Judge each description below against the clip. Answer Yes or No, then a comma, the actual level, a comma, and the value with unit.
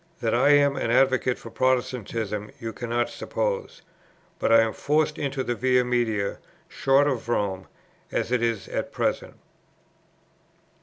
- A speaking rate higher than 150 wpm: No, average, 145 wpm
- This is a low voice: Yes, low, 120 Hz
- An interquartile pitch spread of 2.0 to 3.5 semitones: Yes, average, 2.9 semitones